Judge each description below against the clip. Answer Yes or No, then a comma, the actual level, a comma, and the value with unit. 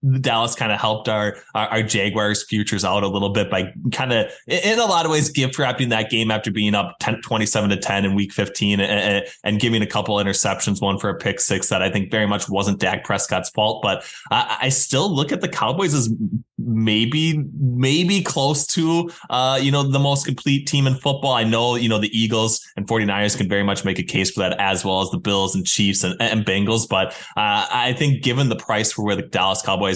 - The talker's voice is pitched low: Yes, low, 110 Hz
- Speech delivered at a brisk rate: Yes, fast, 230 wpm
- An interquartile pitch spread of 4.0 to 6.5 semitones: Yes, average, 4.4 semitones